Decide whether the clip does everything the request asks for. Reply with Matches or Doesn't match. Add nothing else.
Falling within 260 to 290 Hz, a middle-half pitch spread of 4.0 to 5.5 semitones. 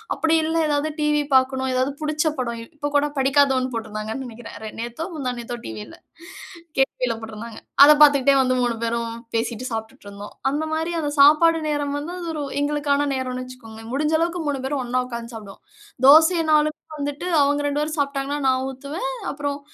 Doesn't match